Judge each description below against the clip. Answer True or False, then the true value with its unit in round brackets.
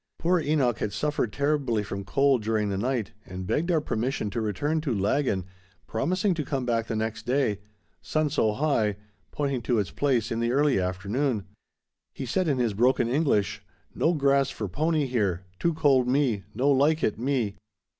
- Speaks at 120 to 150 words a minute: False (175 wpm)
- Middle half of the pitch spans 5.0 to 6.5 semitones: True (5.4 semitones)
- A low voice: True (125 Hz)